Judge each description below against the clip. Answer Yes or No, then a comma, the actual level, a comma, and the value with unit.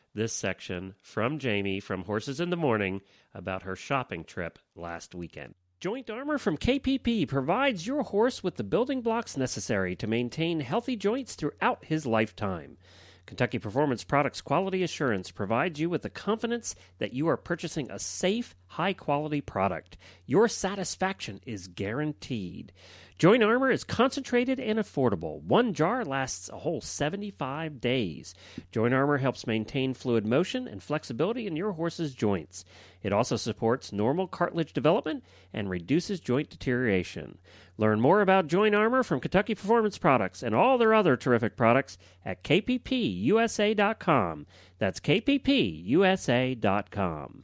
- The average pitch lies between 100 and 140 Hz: Yes, low, 135 Hz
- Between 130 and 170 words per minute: Yes, average, 140 wpm